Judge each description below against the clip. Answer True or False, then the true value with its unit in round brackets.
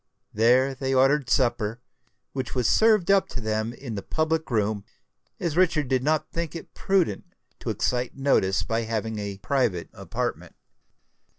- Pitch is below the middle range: True (130 Hz)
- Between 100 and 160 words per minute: True (155 wpm)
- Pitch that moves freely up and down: True (5.9 semitones)